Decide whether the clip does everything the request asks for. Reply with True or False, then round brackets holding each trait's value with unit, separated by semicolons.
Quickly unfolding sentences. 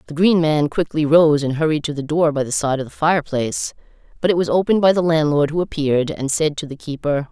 True (245 wpm)